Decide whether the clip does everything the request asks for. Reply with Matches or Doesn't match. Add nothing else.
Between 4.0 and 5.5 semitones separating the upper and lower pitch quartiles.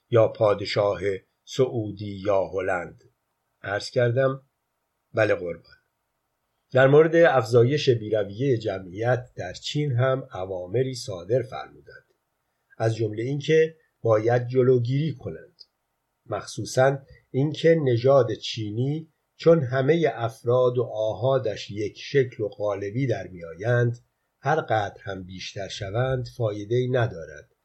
Doesn't match